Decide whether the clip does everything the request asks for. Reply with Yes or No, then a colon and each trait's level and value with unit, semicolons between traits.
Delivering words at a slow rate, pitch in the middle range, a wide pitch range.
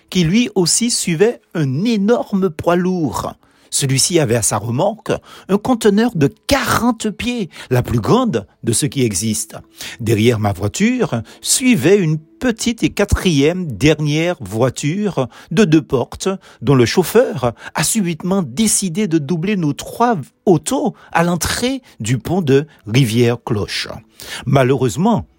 Yes: slow, 130 wpm; medium, 170 Hz; wide, 8.1 semitones